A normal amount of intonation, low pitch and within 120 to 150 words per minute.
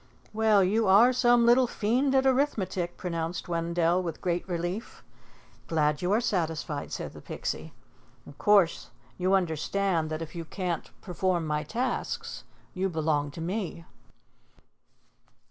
No: average, 4.5 semitones; medium, 180 Hz; slow, 135 wpm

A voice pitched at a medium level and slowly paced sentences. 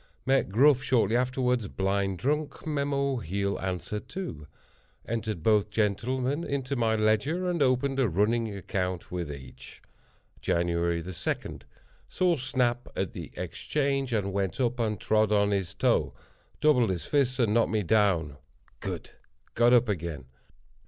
No: low, 110 Hz; slow, 130 wpm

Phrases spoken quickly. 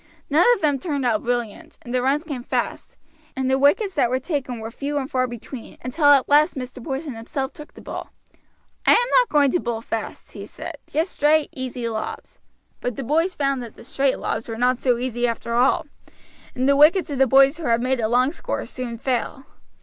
Yes: fast, 215 wpm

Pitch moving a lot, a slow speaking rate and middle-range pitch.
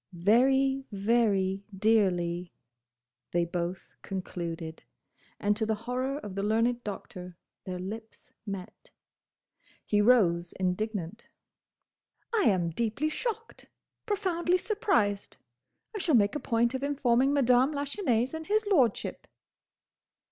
No: wide, 6.1 semitones; slow, 110 wpm; high, 225 Hz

